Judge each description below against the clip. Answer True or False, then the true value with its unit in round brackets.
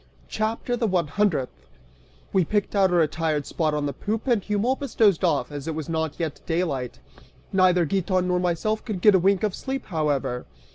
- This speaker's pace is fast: False (190 wpm)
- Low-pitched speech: False (180 Hz)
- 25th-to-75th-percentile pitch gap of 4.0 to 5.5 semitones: True (5.0 semitones)